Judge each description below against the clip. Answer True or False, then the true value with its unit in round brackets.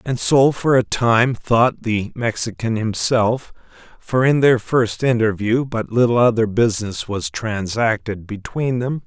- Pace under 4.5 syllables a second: True (4.0 syllables/s)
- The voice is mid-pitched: False (115 Hz)